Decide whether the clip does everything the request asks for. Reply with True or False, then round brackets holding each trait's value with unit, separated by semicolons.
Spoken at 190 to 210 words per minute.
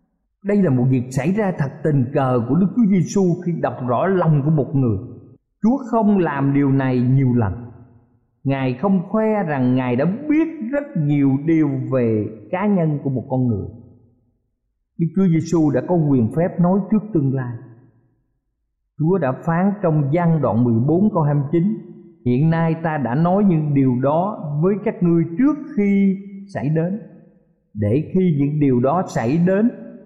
False (170 wpm)